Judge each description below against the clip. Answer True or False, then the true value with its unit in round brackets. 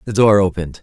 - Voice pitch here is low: True (100 Hz)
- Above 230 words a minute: False (220 wpm)